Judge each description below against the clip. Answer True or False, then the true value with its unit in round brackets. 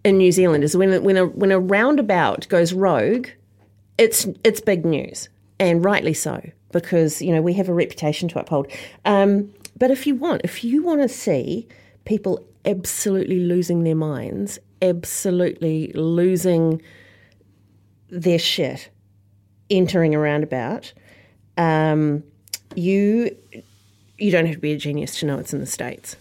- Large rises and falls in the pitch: True (7.4 semitones)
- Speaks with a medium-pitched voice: True (165 Hz)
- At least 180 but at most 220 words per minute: False (150 wpm)